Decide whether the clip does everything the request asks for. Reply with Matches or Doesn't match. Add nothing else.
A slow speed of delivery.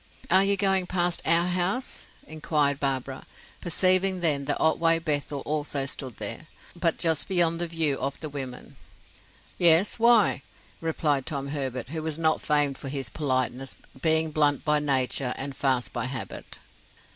Doesn't match